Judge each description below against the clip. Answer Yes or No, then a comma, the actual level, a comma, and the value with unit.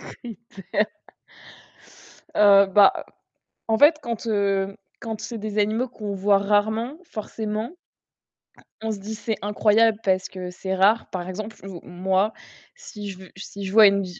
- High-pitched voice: Yes, high, 205 Hz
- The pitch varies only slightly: Yes, narrow, 2.2 semitones